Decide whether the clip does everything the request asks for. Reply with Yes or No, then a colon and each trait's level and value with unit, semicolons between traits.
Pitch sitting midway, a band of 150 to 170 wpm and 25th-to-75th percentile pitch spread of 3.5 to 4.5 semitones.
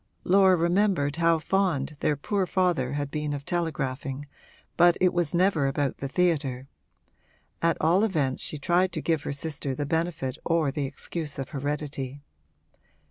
Yes: medium, 155 Hz; average, 155 wpm; average, 3.8 semitones